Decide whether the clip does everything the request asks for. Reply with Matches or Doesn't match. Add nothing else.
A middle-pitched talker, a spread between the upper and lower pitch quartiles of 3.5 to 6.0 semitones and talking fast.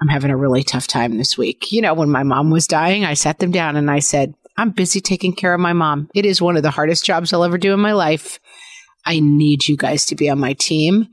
Matches